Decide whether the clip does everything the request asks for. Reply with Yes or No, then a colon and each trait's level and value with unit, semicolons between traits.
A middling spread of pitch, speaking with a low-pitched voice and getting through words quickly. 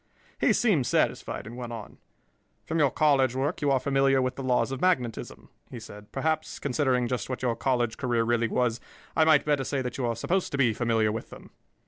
Yes: average, 3.0 semitones; low, 130 Hz; fast, 210 wpm